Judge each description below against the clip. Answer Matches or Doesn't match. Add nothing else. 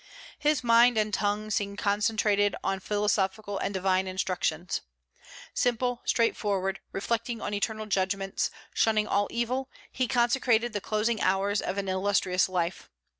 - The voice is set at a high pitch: Matches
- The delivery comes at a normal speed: Doesn't match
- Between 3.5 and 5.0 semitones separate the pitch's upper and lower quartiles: Doesn't match